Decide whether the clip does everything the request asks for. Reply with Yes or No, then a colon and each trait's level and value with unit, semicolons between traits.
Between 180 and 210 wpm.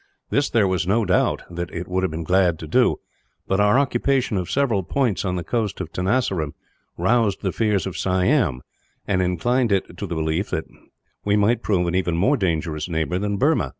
Yes: average, 200 wpm